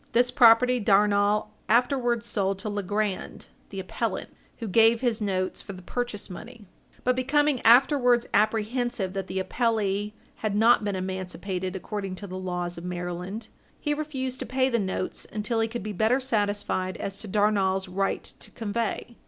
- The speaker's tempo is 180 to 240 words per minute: No, average, 160 wpm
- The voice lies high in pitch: Yes, high, 210 Hz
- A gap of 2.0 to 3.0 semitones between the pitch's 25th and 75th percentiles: No, average, 3.8 semitones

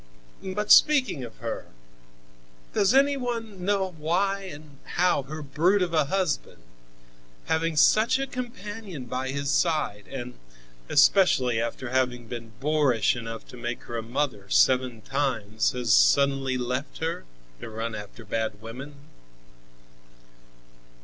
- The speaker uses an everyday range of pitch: No, wide, 7.2 semitones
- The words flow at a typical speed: No, slow, 130 wpm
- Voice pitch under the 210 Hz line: Yes, medium, 140 Hz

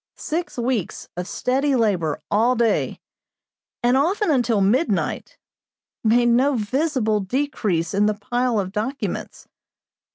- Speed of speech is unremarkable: No, slow, 120 wpm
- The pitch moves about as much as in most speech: Yes, average, 4.1 semitones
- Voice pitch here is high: Yes, high, 240 Hz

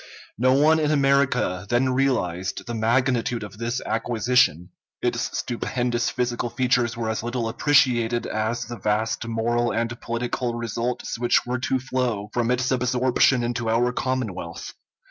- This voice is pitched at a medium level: No, low, 120 Hz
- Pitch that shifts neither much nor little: No, narrow, 2.0 semitones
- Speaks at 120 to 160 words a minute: Yes, average, 145 wpm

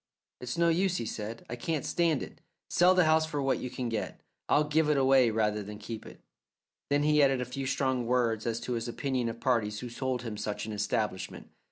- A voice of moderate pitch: No, low, 125 Hz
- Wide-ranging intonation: No, average, 4.5 semitones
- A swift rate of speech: Yes, fast, 225 wpm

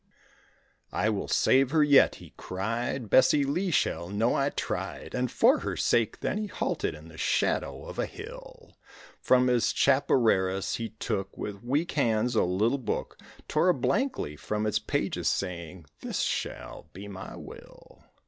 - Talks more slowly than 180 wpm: Yes, average, 165 wpm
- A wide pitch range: Yes, wide, 6.0 semitones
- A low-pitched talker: Yes, low, 115 Hz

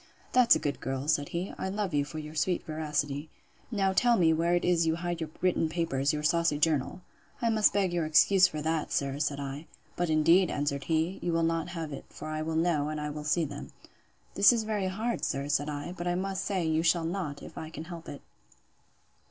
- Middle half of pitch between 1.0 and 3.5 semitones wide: Yes, average, 3.1 semitones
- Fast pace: Yes, fast, 225 wpm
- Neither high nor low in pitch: Yes, medium, 160 Hz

